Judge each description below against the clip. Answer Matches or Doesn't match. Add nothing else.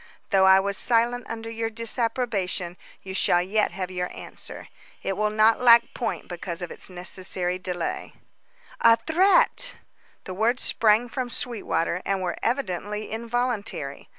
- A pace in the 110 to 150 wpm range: Matches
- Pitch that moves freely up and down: Doesn't match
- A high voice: Matches